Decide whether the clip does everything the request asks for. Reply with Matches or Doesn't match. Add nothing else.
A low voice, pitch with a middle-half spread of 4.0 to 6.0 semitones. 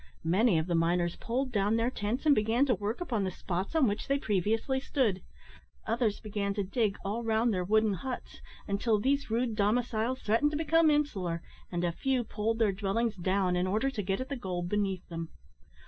Doesn't match